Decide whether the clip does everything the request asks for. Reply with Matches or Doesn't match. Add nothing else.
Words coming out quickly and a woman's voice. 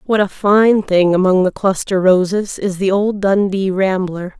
Doesn't match